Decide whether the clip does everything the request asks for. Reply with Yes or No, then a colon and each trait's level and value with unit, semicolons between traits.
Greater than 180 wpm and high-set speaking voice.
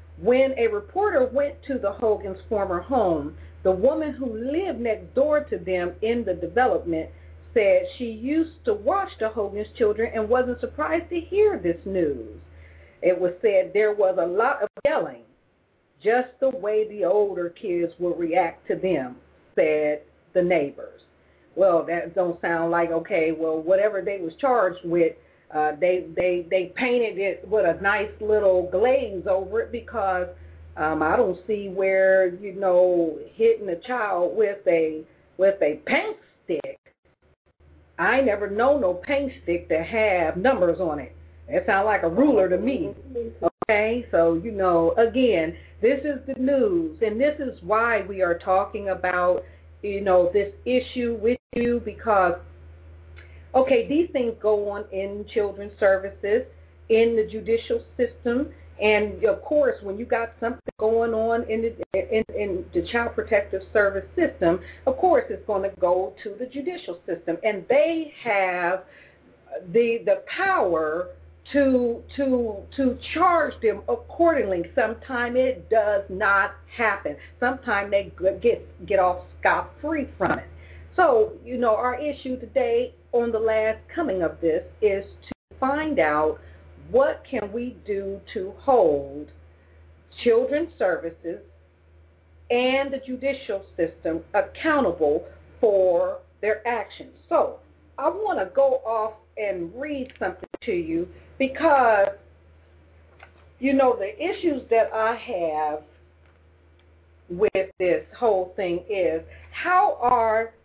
No: average, 145 wpm; high, 210 Hz